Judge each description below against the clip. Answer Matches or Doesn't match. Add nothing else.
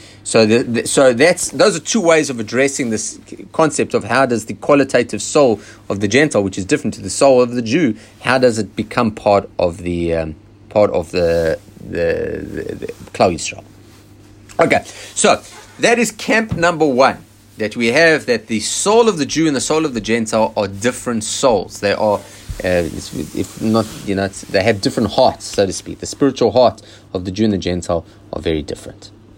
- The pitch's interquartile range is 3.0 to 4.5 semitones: Doesn't match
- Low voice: Matches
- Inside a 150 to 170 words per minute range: Doesn't match